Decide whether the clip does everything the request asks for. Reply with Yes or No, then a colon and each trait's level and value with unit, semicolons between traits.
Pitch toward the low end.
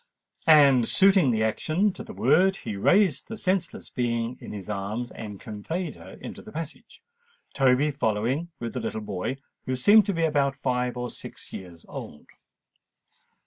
Yes: low, 130 Hz